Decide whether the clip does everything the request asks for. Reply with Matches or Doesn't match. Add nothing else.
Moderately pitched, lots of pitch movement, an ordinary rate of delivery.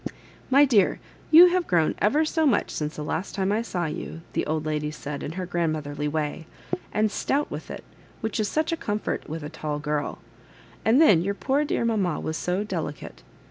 Doesn't match